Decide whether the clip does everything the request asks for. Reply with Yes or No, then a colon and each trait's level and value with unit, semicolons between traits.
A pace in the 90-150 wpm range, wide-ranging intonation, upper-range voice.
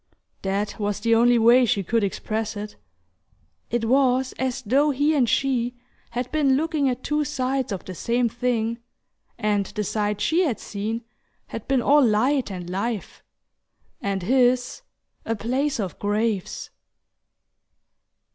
No: average, 145 wpm; average, 3.8 semitones; high, 235 Hz